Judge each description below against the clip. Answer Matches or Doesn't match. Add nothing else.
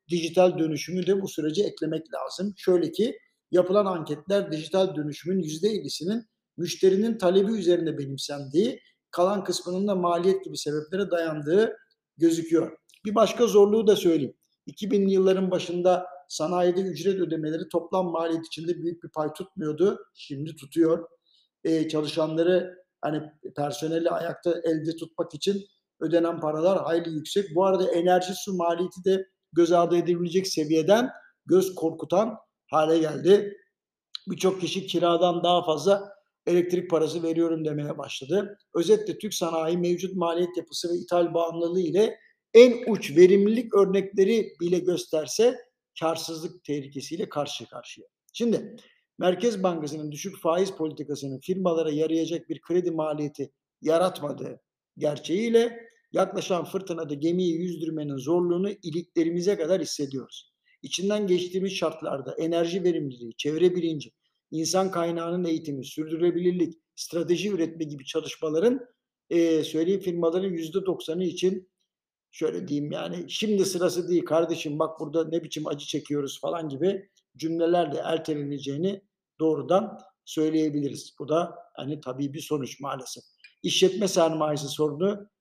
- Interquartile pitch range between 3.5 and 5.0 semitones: Doesn't match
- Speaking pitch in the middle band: Matches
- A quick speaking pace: Doesn't match